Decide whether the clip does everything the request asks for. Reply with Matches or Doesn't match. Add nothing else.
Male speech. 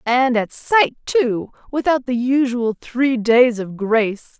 Doesn't match